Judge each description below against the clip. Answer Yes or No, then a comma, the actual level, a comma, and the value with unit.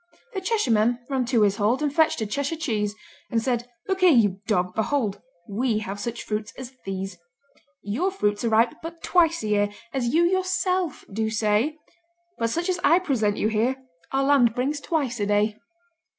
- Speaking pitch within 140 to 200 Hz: No, high, 240 Hz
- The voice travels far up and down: Yes, wide, 6.5 semitones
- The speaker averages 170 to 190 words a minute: Yes, average, 185 wpm